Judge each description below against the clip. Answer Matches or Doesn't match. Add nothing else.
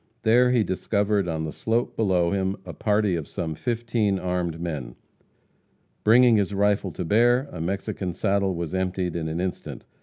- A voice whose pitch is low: Matches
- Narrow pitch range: Doesn't match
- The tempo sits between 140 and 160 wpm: Doesn't match